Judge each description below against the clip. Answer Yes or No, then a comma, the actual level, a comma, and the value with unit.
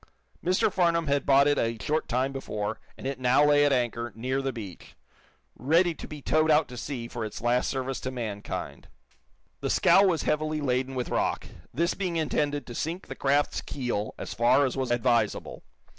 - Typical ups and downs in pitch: Yes, average, 3.9 semitones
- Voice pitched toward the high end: No, low, 135 Hz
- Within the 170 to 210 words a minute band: Yes, average, 190 wpm